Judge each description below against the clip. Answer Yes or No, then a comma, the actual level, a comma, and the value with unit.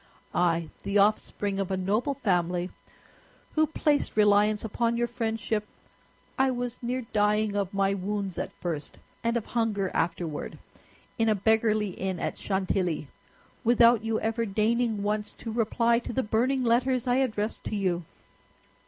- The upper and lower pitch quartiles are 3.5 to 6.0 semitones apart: No, average, 3.1 semitones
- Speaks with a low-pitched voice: No, high, 215 Hz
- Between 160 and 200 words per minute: No, average, 145 wpm